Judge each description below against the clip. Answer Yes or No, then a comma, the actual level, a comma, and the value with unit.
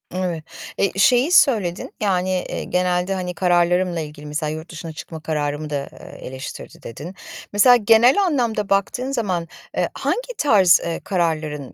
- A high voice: No, medium, 180 Hz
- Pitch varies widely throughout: No, average, 4.9 semitones